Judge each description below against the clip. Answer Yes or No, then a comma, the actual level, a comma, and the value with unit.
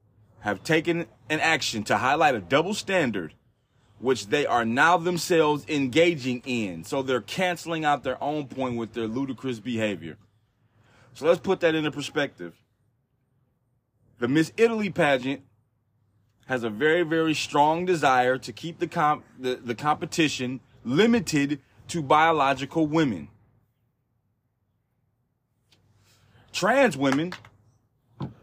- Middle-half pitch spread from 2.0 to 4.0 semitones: No, average, 4.9 semitones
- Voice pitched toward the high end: No, low, 130 Hz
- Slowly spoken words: Yes, slow, 120 wpm